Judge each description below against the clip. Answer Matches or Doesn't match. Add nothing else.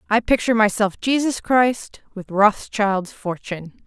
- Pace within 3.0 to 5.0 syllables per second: Matches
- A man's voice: Doesn't match